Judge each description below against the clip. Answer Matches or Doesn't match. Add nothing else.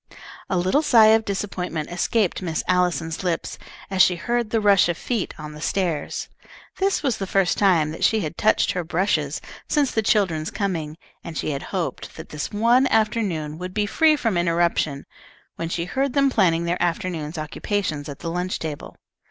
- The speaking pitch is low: Doesn't match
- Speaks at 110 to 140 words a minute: Doesn't match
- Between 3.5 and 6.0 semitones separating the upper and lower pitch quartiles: Matches